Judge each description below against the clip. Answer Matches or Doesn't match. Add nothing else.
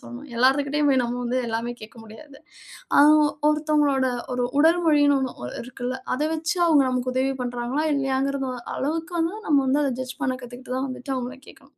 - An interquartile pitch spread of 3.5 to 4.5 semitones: Doesn't match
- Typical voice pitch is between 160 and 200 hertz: Doesn't match